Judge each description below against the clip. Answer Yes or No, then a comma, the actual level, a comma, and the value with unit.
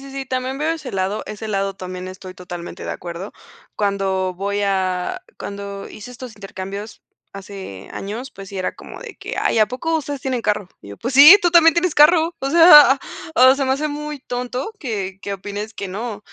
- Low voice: No, high, 215 Hz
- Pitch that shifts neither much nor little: No, wide, 5.9 semitones